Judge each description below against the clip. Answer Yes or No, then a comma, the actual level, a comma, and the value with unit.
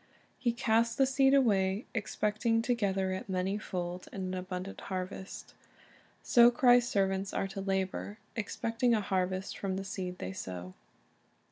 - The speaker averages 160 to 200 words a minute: No, average, 150 wpm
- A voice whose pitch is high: Yes, high, 195 Hz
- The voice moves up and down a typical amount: Yes, average, 3.5 semitones